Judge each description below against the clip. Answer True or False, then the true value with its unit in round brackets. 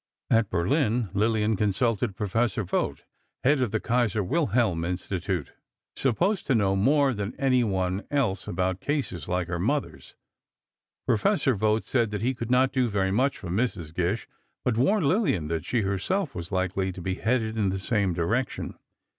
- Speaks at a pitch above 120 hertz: False (110 Hz)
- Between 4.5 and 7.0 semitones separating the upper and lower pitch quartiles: True (5.1 semitones)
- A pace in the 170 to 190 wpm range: False (160 wpm)